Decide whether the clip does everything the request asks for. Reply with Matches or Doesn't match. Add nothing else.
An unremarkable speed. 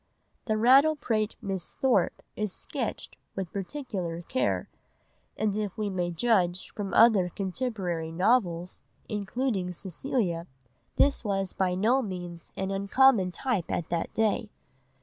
Doesn't match